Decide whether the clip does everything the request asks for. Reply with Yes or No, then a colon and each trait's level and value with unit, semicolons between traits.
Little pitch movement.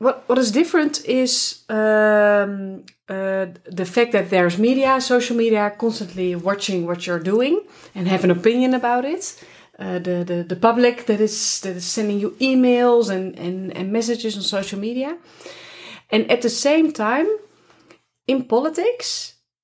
No: average, 4.9 semitones